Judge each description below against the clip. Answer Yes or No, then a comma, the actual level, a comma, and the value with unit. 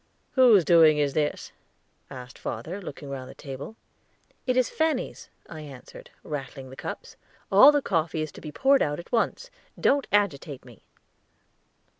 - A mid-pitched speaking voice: Yes, medium, 155 Hz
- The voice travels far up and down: Yes, wide, 8.3 semitones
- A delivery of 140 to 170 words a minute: Yes, average, 150 wpm